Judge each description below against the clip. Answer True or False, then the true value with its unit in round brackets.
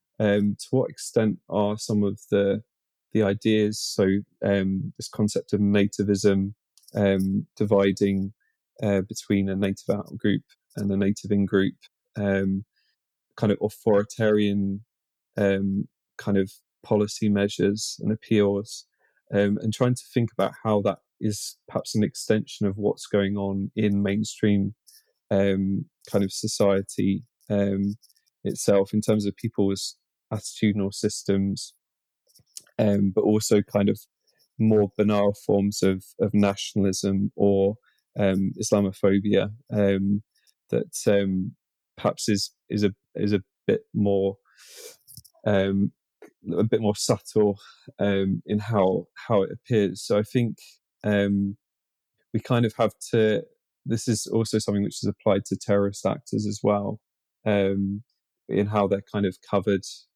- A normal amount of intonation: False (1.4 semitones)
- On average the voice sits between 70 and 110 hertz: True (100 Hz)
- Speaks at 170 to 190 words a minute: False (135 wpm)